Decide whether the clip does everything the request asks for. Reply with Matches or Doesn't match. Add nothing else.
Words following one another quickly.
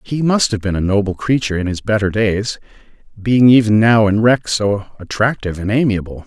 Doesn't match